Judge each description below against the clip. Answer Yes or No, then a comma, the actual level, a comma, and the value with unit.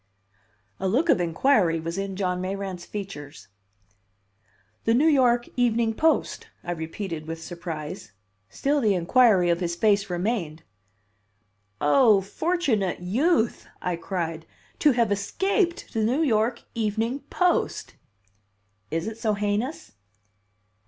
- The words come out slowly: Yes, slow, 120 wpm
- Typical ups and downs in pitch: No, wide, 5.7 semitones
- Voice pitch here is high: Yes, high, 205 Hz